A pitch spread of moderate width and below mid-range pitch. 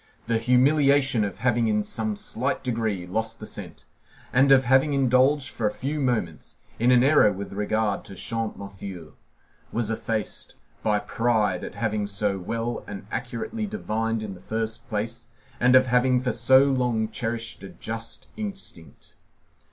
Yes: average, 3.3 semitones; low, 115 Hz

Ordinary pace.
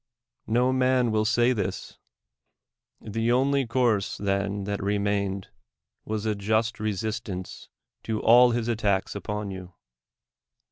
No: slow, 120 wpm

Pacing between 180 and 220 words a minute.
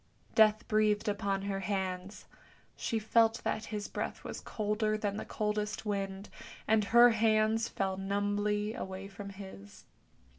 No: average, 140 wpm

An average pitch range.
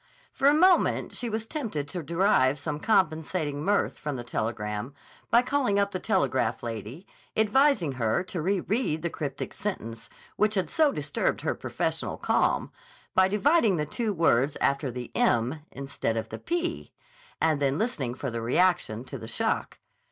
No: wide, 8.3 semitones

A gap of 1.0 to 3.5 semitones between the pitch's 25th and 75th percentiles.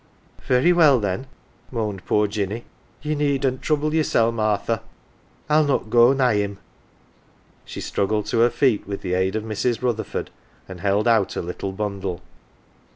No: average, 4.4 semitones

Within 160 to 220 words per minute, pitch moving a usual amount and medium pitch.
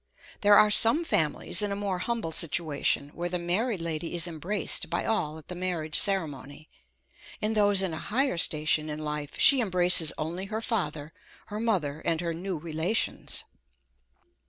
Yes: average, 165 wpm; average, 4.7 semitones; medium, 175 Hz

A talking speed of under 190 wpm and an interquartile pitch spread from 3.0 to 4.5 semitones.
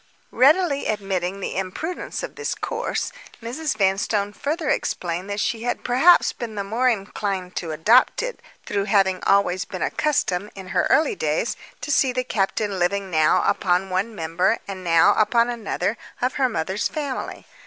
No: average, 165 wpm; average, 5.1 semitones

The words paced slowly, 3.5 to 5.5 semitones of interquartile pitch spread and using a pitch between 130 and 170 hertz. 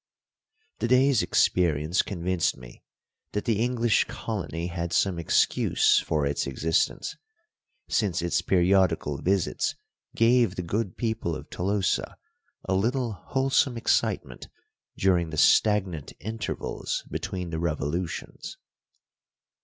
No: slow, 105 wpm; average, 4.8 semitones; very low, 90 Hz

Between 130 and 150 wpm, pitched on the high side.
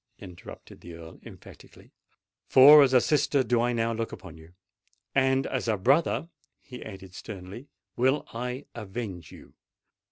No: average, 140 wpm; low, 115 Hz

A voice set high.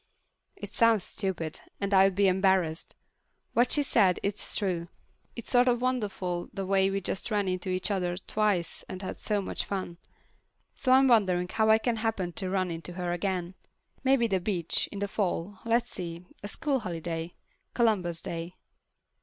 Yes: high, 195 Hz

